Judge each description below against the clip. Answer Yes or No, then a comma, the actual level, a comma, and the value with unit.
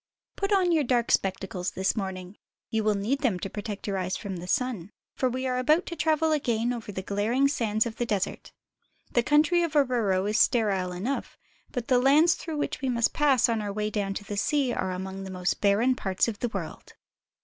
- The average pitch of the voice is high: Yes, high, 225 Hz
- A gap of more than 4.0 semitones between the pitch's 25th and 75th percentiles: Yes, average, 5.2 semitones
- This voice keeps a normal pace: No, fast, 215 wpm